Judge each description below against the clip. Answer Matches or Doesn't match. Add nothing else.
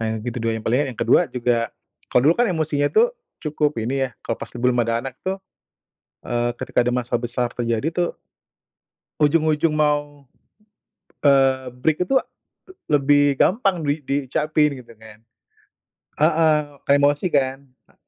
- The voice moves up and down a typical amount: Matches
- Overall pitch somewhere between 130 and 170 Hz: Matches